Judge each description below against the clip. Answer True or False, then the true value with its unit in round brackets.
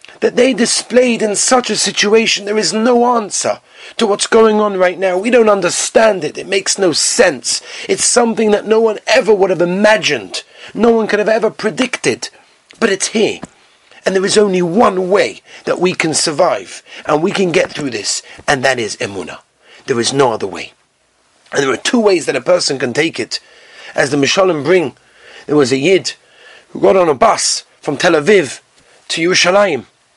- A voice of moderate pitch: False (210 Hz)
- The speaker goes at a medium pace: True (195 wpm)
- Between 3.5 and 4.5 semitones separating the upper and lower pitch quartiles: True (4.1 semitones)